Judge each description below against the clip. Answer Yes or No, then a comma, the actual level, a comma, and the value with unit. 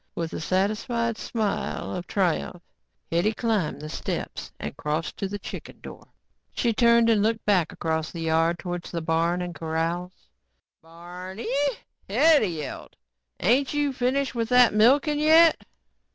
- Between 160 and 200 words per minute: No, average, 145 wpm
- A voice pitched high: Yes, high, 200 Hz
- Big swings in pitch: Yes, wide, 5.9 semitones